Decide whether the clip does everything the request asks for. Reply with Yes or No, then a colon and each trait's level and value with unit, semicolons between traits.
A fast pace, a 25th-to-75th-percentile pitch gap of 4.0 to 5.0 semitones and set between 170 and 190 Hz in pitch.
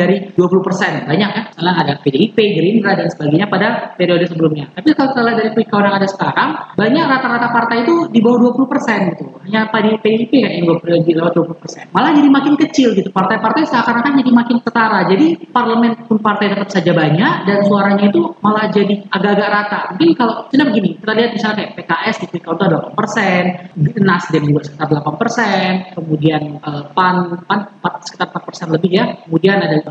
No: fast, 195 wpm; average, 4.7 semitones; high, 200 Hz